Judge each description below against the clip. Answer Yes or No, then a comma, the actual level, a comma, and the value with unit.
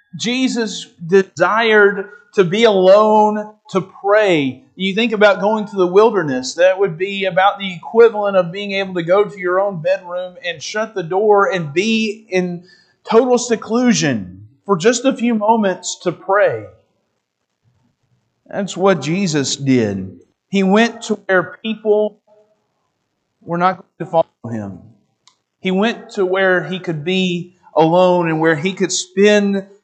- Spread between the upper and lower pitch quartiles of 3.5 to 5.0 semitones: No, average, 3.0 semitones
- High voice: Yes, high, 195 Hz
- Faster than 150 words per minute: No, average, 145 wpm